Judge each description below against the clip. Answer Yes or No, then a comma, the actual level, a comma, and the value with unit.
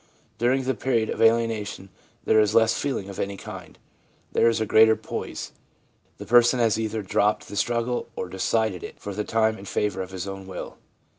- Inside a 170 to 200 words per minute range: Yes, average, 190 wpm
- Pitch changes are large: No, narrow, 2.6 semitones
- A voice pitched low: Yes, low, 110 Hz